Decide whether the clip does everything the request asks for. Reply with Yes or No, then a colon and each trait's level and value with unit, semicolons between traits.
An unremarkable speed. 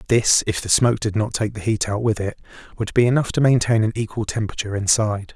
No: fast, 235 wpm